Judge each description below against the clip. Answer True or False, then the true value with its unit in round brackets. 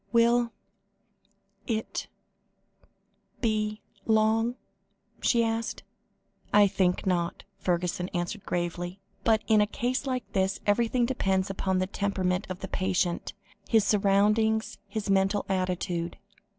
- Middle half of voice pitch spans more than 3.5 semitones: False (3.1 semitones)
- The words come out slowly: True (110 wpm)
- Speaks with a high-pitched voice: True (200 Hz)